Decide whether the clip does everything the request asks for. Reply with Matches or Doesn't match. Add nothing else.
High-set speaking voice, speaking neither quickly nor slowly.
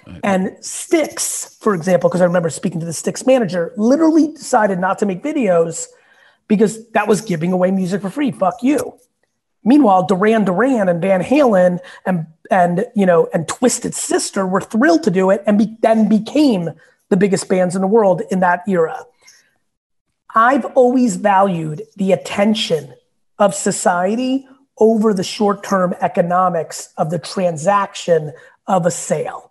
Matches